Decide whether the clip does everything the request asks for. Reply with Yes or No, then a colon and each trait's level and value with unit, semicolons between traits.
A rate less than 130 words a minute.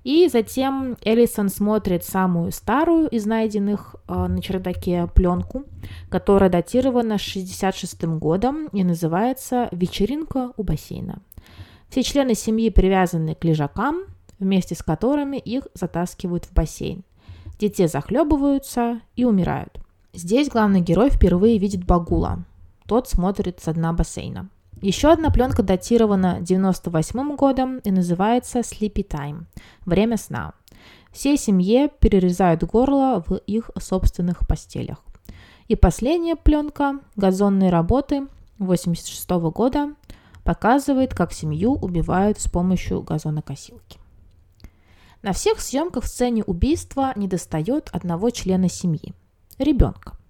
Yes: slow, 110 wpm